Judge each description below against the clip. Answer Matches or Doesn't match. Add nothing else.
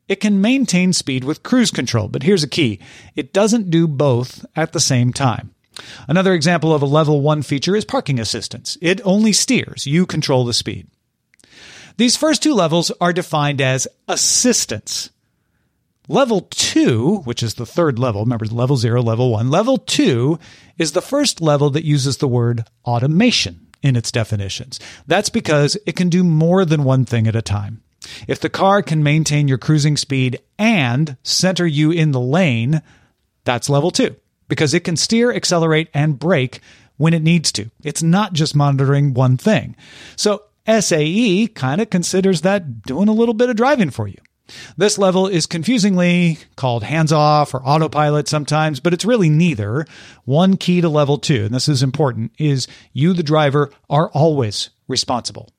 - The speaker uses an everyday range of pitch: Doesn't match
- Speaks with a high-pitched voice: Doesn't match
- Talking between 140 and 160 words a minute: Doesn't match